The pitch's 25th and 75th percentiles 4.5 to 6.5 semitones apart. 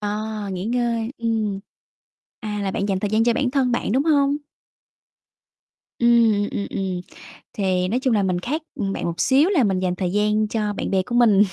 No: average, 3.7 semitones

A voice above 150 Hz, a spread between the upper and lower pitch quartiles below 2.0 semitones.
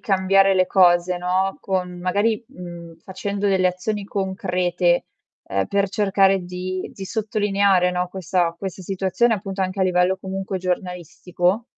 Yes: medium, 185 Hz; narrow, 1.5 semitones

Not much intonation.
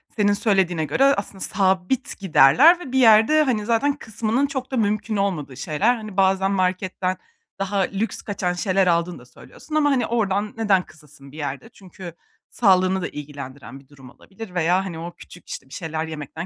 No: average, 4.9 semitones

